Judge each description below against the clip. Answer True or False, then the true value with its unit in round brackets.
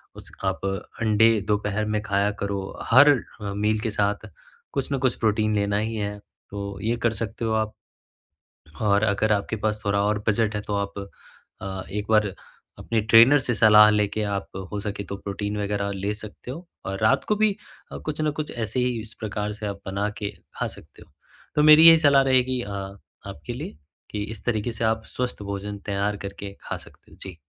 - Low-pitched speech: True (105 Hz)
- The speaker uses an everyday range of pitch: False (2.0 semitones)